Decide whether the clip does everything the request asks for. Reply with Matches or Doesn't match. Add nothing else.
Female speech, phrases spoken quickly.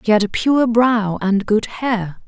Matches